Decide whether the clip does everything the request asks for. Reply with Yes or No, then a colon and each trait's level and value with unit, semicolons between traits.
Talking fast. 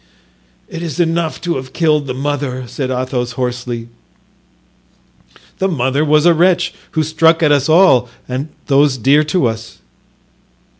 No: average, 150 wpm